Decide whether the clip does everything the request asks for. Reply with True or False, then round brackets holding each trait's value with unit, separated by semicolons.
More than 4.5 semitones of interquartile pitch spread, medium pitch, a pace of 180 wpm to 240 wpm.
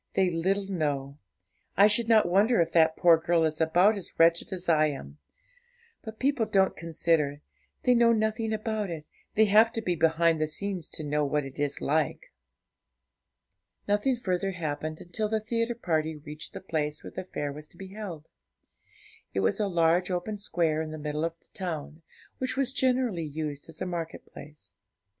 True (5.2 semitones; 170 Hz; 185 wpm)